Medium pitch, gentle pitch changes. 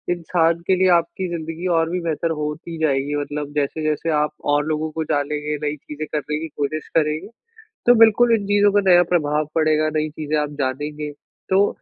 Yes: medium, 155 Hz; narrow, 2.2 semitones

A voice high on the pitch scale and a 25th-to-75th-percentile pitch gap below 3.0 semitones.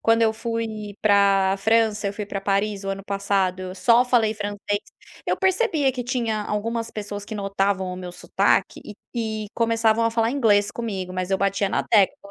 Yes: high, 210 Hz; narrow, 2.5 semitones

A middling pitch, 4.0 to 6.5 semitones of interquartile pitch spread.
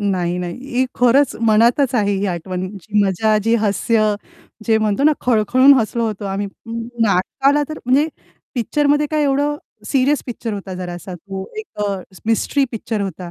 No: high, 220 Hz; average, 4.7 semitones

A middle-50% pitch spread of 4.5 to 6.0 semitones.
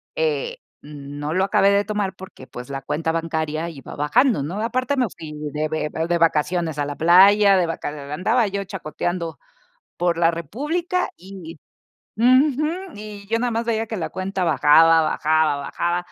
Yes: average, 5.1 semitones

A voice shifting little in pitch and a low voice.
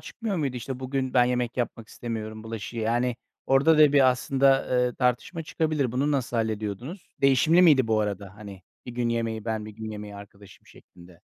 No: average, 3.9 semitones; low, 120 Hz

